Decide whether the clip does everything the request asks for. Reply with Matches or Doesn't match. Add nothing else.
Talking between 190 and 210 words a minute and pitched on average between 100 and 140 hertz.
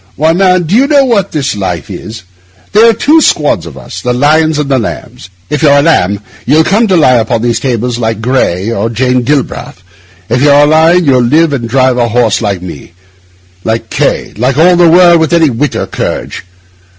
Matches